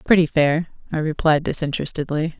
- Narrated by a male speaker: No, female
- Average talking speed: No, slow, 125 wpm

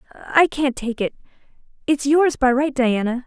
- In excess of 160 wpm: No, average, 145 wpm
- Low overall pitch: No, very high, 265 Hz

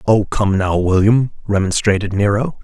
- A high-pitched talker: No, low, 100 Hz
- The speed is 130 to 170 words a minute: Yes, slow, 135 wpm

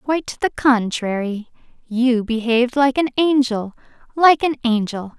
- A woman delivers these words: Yes, female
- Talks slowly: Yes, slow, 125 wpm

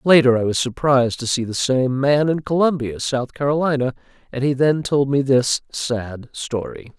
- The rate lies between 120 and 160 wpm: No, average, 180 wpm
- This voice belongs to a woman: No, male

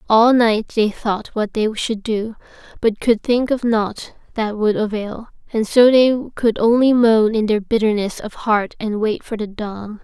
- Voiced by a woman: Yes, female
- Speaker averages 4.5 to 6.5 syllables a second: No, 4.1 syllables/s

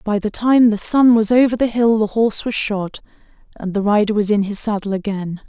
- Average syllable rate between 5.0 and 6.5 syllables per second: Yes, 5.4 syllables/s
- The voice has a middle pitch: No, high, 215 Hz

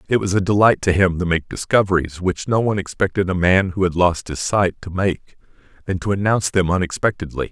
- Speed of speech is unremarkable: No, fast, 215 wpm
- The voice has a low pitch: Yes, very low, 95 Hz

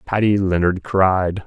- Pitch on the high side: No, very low, 95 Hz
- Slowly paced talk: Yes, slow, 125 wpm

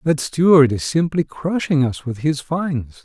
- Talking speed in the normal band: Yes, average, 180 wpm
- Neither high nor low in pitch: Yes, medium, 145 Hz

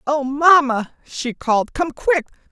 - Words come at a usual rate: Yes, average, 145 wpm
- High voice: Yes, very high, 280 Hz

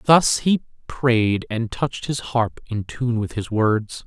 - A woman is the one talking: No, male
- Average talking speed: Yes, average, 175 wpm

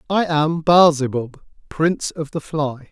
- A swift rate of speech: No, average, 165 wpm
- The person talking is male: Yes, male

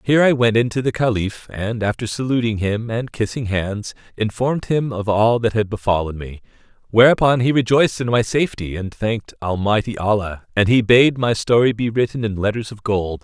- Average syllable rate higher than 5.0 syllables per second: Yes, 5.4 syllables/s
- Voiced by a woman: No, male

